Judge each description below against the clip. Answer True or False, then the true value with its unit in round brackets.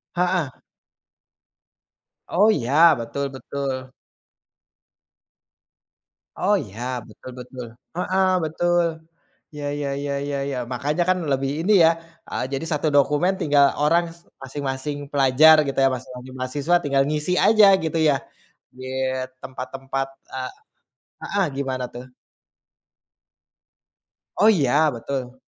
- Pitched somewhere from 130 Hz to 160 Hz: True (140 Hz)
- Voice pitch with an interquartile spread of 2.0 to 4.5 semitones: True (3.5 semitones)